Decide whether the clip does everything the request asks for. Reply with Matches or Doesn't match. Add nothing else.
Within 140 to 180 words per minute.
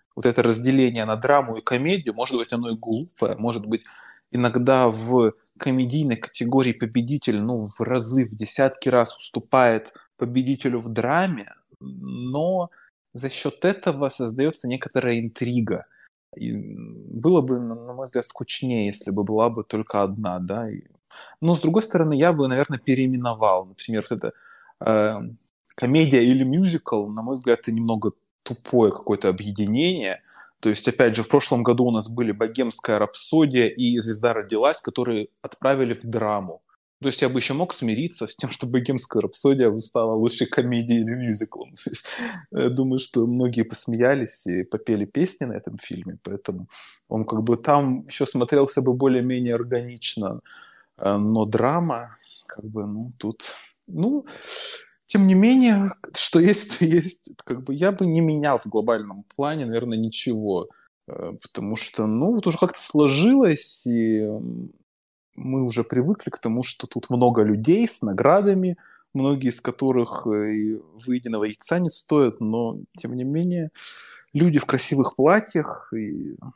Matches